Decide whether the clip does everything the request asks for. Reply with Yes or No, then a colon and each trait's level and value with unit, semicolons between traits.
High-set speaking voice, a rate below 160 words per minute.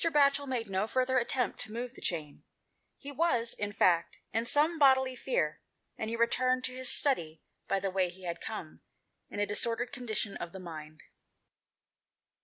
No: high, 230 Hz; average, 170 wpm